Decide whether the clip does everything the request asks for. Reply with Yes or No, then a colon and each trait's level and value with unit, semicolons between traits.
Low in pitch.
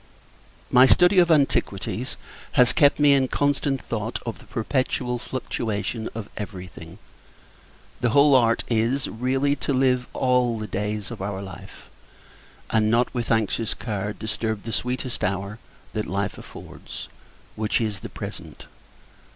Yes: low, 115 Hz